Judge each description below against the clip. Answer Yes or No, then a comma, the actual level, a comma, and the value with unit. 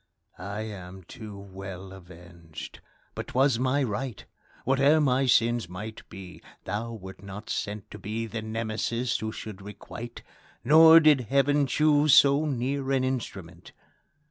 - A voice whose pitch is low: Yes, low, 115 Hz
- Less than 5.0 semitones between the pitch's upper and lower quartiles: No, wide, 5.6 semitones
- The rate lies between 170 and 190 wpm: No, average, 140 wpm